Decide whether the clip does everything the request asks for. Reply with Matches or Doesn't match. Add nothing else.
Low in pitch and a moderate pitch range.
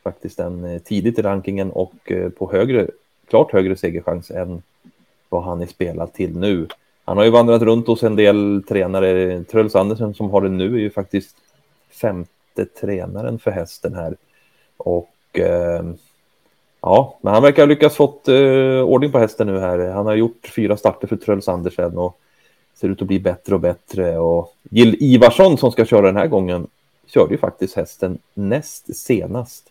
Matches